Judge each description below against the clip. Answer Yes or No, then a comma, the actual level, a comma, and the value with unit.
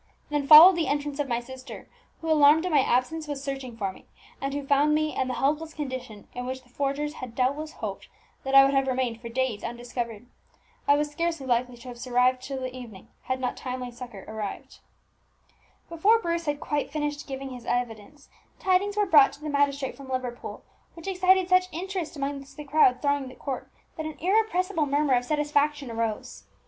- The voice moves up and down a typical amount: Yes, average, 3.3 semitones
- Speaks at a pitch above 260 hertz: Yes, very high, 275 Hz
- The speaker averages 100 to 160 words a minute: No, average, 195 wpm